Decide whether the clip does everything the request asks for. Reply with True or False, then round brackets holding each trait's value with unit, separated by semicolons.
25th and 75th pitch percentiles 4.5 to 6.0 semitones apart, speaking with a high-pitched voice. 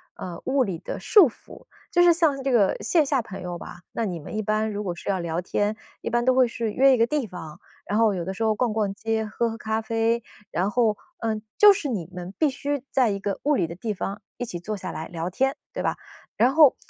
True (5.1 semitones; 220 Hz)